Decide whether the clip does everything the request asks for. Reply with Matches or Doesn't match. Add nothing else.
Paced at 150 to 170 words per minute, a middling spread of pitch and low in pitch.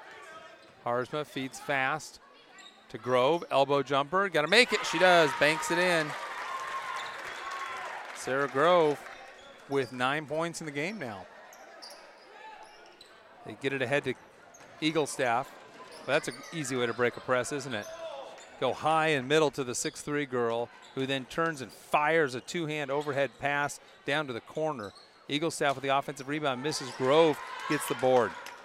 Doesn't match